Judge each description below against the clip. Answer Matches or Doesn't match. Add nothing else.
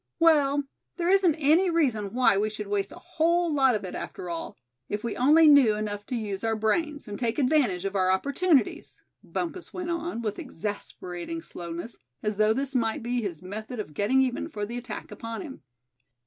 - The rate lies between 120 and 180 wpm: Doesn't match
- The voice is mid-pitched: Doesn't match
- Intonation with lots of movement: Matches